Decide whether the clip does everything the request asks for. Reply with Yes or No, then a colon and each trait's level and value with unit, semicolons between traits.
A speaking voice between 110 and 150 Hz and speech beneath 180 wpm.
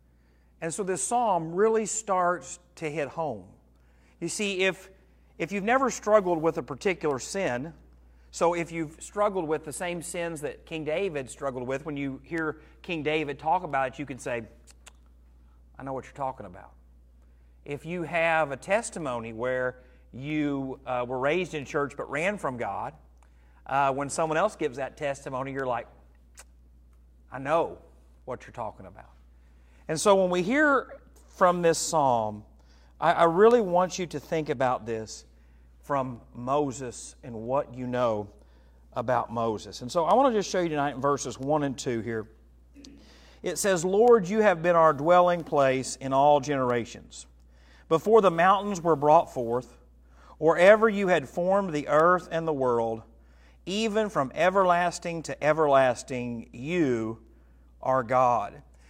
Yes: medium, 140 Hz; average, 160 wpm